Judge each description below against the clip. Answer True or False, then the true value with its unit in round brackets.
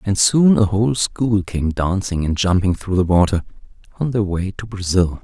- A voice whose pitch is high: False (100 Hz)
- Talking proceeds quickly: False (195 wpm)